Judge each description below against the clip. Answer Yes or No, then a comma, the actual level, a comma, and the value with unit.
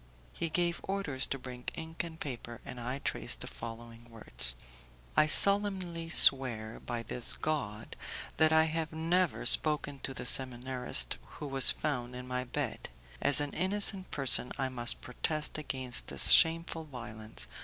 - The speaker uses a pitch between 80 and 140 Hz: Yes, low, 135 Hz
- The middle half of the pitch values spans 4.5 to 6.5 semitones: Yes, average, 4.8 semitones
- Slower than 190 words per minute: Yes, average, 155 wpm